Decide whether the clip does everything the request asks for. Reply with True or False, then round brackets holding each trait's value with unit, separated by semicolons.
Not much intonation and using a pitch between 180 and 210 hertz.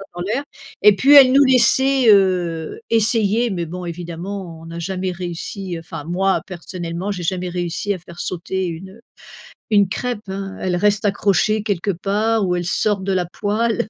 False (3.2 semitones; 190 Hz)